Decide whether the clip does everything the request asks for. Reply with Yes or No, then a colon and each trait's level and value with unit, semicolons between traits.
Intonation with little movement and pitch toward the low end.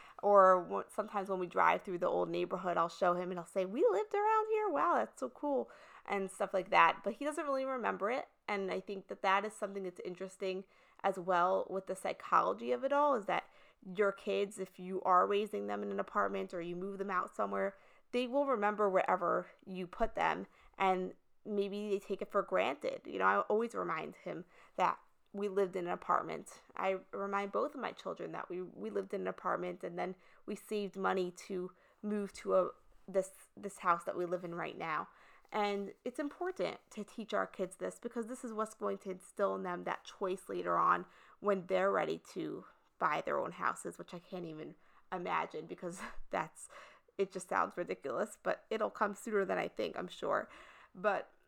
No: narrow, 2.3 semitones; high, 195 Hz